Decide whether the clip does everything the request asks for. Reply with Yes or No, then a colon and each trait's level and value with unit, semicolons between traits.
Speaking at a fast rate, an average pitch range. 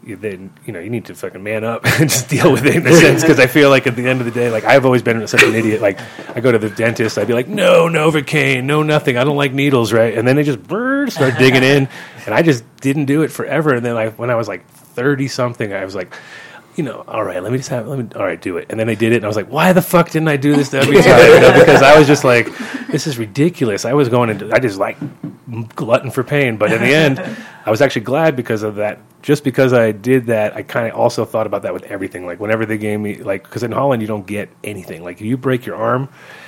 Yes: fast, 285 wpm; average, 4.5 semitones